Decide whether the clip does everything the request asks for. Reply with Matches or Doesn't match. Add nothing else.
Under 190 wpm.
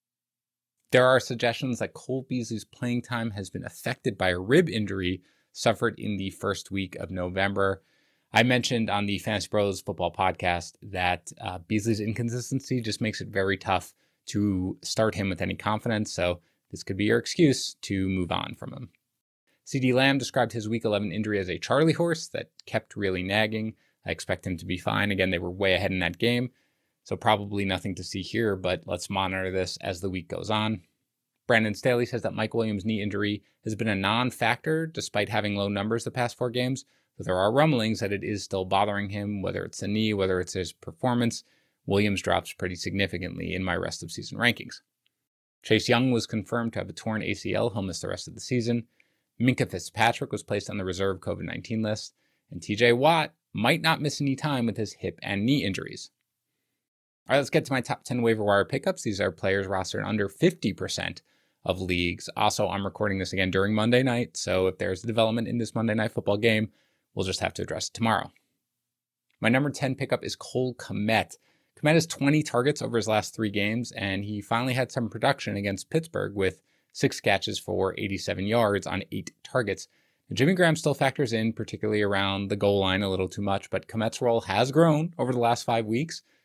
Doesn't match